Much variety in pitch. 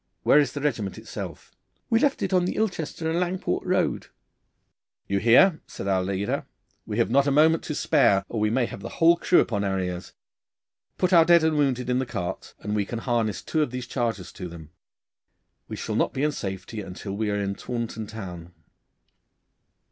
Yes: wide, 7.8 semitones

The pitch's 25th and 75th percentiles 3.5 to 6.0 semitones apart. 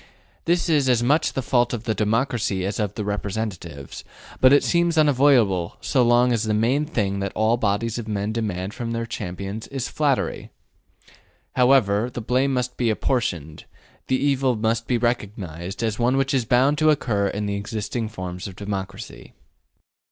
Yes: average, 4.1 semitones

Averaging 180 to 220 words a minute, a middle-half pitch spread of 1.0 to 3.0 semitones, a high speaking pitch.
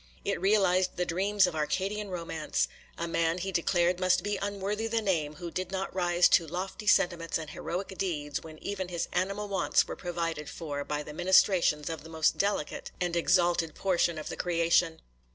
No: average, 185 wpm; narrow, 2.6 semitones; medium, 175 Hz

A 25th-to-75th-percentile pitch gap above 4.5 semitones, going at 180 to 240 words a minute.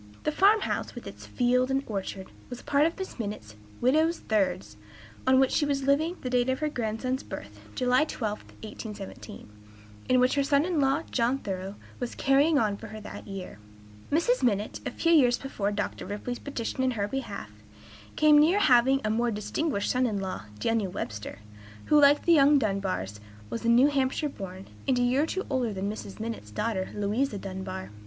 Yes: wide, 5.5 semitones; average, 190 wpm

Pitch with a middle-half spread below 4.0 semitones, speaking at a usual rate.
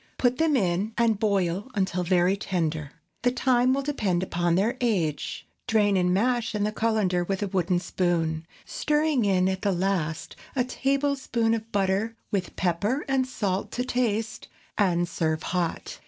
No: average, 4.9 semitones; average, 160 wpm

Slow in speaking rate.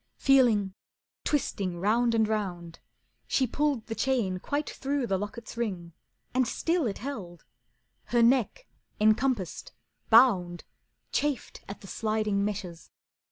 Yes: slow, 120 wpm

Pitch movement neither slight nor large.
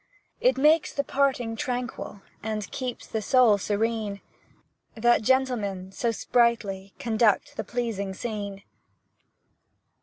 Yes: average, 3.6 semitones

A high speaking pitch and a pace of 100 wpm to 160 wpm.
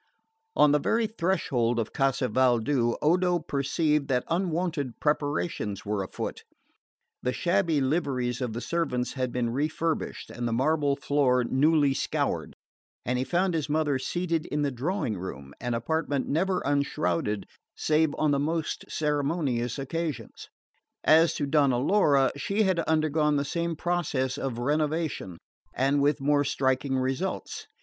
No: medium, 145 Hz; average, 140 wpm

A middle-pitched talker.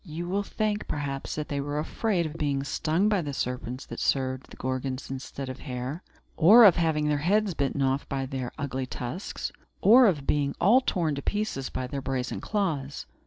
Yes: medium, 145 Hz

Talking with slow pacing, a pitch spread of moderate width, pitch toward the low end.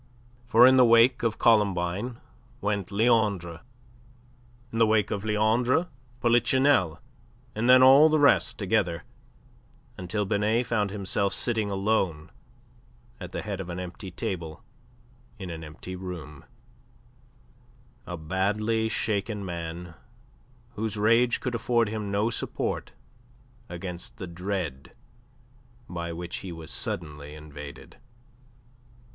Yes: slow, 115 wpm; average, 4.6 semitones; low, 100 Hz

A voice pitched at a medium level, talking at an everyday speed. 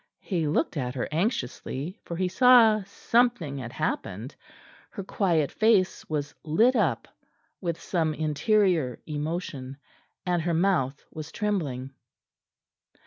No: medium, 165 Hz; slow, 120 wpm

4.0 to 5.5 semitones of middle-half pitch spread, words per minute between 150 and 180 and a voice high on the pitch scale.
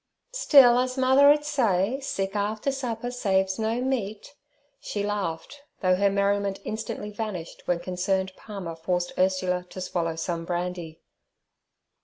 No: average, 5.1 semitones; average, 140 wpm; high, 200 Hz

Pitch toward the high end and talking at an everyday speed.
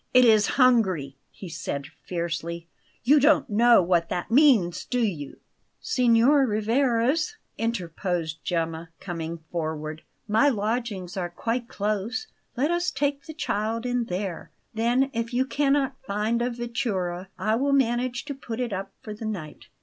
Yes: high, 225 Hz; average, 150 wpm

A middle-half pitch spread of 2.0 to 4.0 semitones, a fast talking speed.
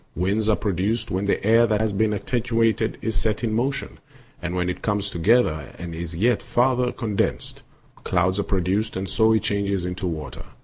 No: average, 3.6 semitones; average, 185 wpm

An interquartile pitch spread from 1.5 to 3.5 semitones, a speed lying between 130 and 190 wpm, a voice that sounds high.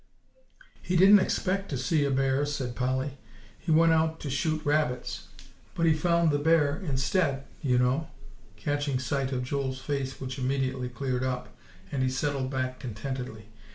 No: average, 3.1 semitones; average, 160 wpm; low, 135 Hz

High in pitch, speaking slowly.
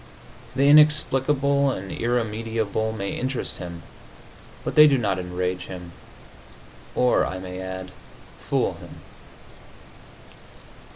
No: low, 110 Hz; slow, 105 wpm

